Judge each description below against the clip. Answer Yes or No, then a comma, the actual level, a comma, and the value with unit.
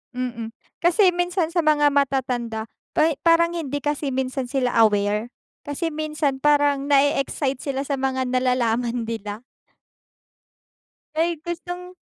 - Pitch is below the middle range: No, very high, 275 Hz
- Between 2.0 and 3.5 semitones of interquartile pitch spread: No, average, 4.0 semitones